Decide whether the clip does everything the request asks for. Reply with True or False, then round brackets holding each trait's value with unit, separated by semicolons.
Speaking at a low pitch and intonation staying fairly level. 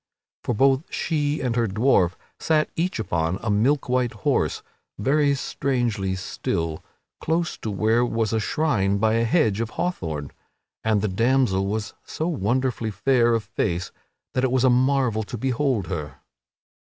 False (115 Hz; 4.8 semitones)